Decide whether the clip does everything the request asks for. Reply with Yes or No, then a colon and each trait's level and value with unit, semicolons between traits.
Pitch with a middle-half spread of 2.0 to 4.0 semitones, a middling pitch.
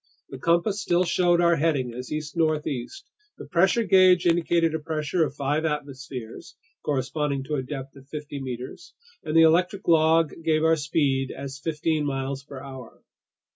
Yes: average, 3.3 semitones; medium, 150 Hz